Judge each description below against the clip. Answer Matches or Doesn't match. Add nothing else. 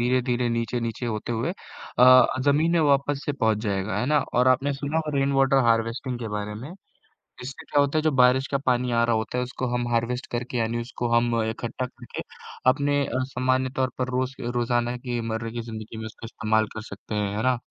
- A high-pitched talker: Doesn't match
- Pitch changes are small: Matches